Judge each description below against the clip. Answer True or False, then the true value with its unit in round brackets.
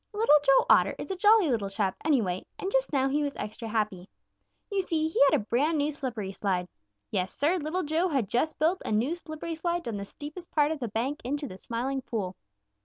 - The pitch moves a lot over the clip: True (6.6 semitones)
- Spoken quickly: True (220 wpm)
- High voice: True (285 Hz)